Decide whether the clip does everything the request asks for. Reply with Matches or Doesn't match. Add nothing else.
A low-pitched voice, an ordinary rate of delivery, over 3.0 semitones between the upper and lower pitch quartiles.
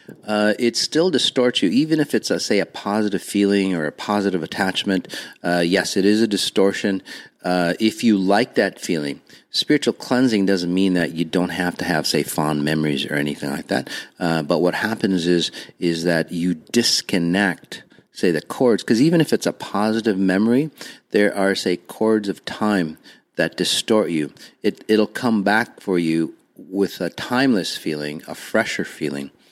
Matches